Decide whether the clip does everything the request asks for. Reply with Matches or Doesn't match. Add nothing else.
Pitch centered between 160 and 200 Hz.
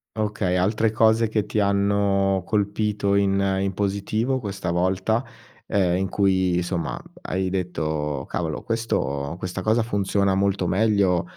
Doesn't match